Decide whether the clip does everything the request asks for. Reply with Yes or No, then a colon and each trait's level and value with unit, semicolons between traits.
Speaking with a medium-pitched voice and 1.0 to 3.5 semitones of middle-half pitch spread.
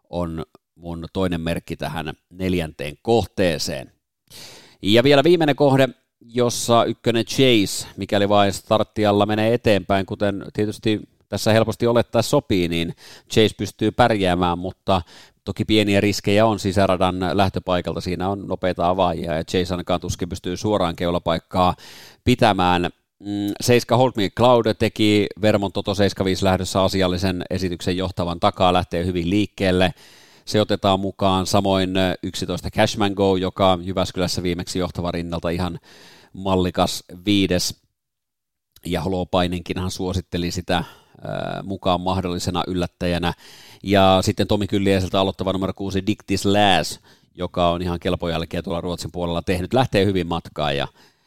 No: very low, 95 Hz; narrow, 2.5 semitones